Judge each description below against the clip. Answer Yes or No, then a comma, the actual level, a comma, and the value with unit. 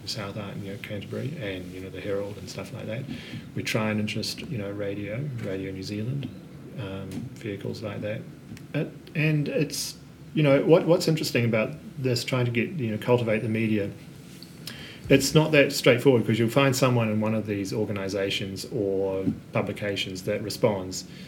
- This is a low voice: Yes, low, 110 Hz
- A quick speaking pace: No, average, 175 wpm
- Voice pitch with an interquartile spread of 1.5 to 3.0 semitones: No, average, 5.3 semitones